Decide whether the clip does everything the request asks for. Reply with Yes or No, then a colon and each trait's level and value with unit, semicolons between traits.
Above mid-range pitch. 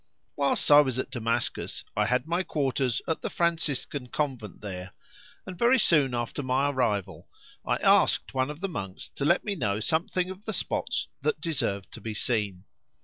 No: low, 135 Hz